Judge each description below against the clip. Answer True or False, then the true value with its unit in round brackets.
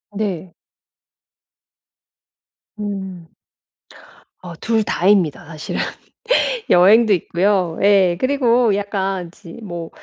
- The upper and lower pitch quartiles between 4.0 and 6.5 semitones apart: False (3.2 semitones)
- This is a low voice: False (195 Hz)